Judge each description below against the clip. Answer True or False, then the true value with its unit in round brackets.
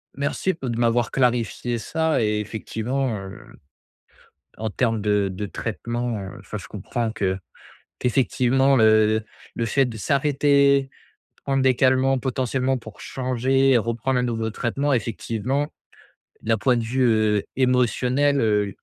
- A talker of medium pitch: False (120 Hz)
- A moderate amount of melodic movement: True (3.2 semitones)